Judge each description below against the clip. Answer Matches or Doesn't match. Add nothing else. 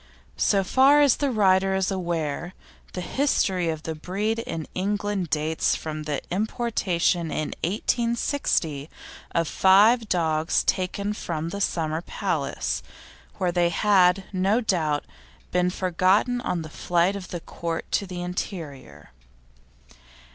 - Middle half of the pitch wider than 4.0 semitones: Doesn't match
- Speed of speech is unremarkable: Doesn't match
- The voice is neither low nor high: Matches